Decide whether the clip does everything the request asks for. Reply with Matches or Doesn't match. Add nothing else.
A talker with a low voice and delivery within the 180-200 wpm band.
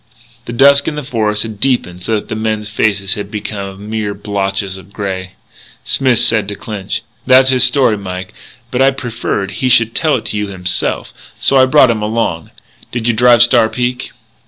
Matches